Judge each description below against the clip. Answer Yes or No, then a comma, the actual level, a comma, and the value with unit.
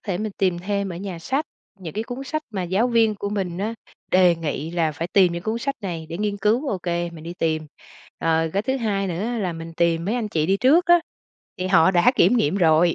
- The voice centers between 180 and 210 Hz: Yes, high, 190 Hz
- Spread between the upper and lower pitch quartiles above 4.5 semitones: No, average, 4.2 semitones